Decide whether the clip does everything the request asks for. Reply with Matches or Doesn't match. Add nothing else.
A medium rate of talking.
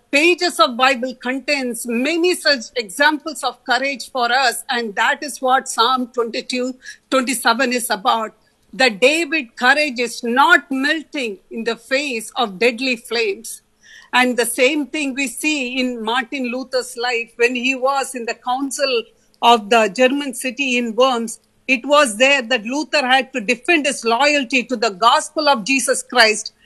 Matches